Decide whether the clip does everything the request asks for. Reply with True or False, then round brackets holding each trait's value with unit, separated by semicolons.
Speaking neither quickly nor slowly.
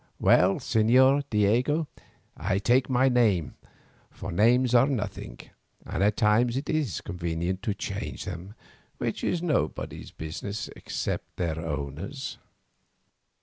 False (120 wpm)